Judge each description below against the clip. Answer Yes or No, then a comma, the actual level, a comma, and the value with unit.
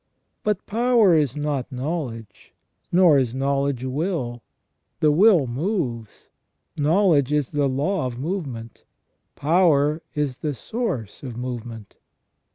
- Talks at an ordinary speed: No, slow, 115 wpm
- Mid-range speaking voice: Yes, medium, 145 Hz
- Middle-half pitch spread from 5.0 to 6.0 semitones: Yes, average, 5.3 semitones